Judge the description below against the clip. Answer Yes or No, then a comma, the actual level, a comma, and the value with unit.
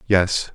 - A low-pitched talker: Yes, very low, 95 Hz